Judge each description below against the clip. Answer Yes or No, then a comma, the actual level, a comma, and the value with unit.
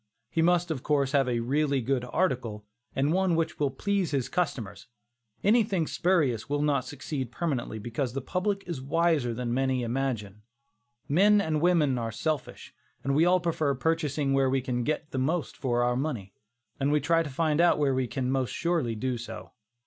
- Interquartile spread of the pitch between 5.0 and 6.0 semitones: No, average, 4.5 semitones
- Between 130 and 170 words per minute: No, average, 185 wpm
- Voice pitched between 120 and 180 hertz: Yes, medium, 140 Hz